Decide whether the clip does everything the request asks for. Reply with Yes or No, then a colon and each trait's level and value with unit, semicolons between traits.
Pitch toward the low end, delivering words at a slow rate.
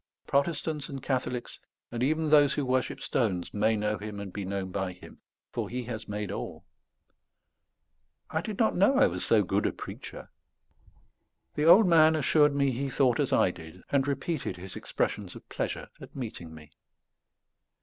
No: low, 125 Hz; average, 170 wpm